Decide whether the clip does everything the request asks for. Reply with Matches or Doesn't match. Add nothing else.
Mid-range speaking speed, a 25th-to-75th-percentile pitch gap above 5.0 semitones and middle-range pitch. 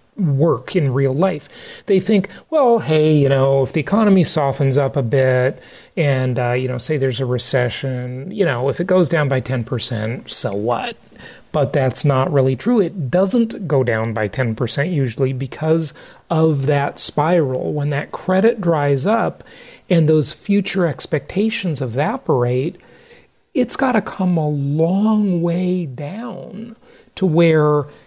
Matches